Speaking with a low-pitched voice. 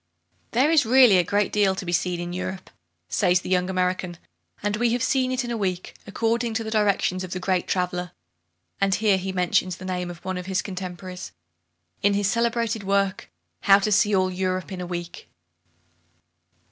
No: high, 190 Hz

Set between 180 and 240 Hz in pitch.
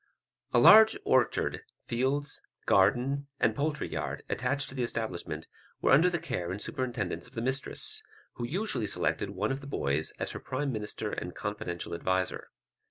No: low, 120 Hz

